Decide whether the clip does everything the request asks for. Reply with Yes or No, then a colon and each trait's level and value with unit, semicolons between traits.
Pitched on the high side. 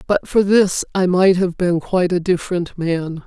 No: medium, 180 Hz